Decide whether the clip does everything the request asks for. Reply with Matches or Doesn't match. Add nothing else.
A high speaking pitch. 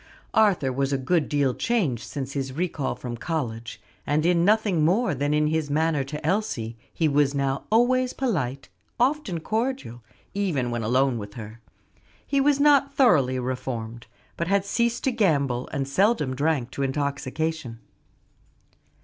Doesn't match